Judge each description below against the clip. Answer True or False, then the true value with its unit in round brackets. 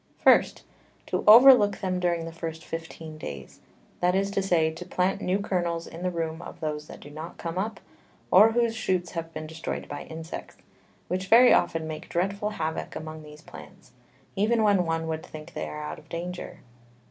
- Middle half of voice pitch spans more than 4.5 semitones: False (3.2 semitones)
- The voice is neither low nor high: True (170 Hz)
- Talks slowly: False (195 wpm)